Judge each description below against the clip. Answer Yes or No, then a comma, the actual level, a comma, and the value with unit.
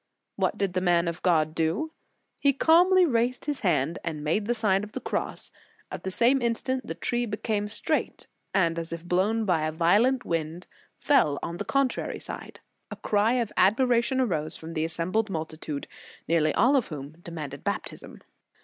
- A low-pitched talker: No, high, 190 Hz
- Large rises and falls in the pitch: Yes, wide, 6.4 semitones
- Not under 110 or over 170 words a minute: No, average, 180 wpm